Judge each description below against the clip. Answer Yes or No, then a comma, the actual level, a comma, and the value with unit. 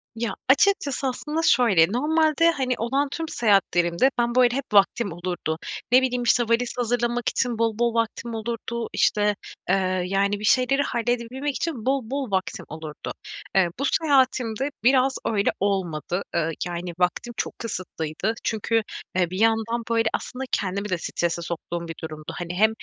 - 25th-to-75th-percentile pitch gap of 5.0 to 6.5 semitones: Yes, average, 5.3 semitones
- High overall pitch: Yes, high, 230 Hz